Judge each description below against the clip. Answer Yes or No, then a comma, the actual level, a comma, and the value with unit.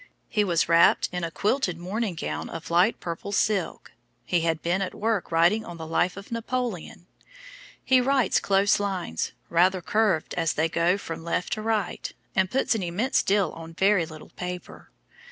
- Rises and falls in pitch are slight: No, average, 4.0 semitones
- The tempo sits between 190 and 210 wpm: No, average, 175 wpm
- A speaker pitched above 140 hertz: Yes, medium, 185 Hz